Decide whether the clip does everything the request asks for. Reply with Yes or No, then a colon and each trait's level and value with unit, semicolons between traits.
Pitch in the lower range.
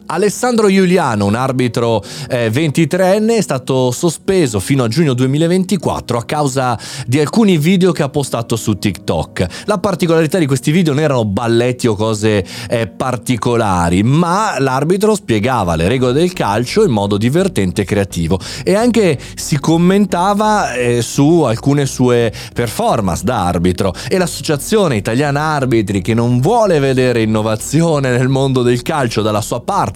Yes: low, 130 Hz